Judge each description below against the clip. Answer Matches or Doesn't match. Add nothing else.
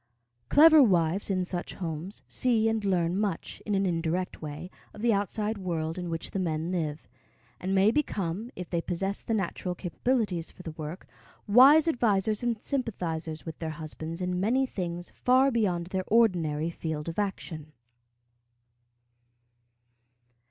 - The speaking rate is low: Doesn't match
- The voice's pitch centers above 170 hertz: Matches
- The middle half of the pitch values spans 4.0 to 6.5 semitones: Matches